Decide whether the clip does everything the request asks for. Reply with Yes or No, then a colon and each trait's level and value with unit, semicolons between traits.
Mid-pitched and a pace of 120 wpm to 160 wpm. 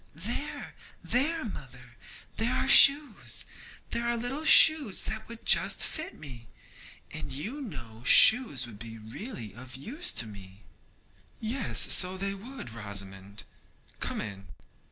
Yes: medium, 180 Hz; slow, 135 wpm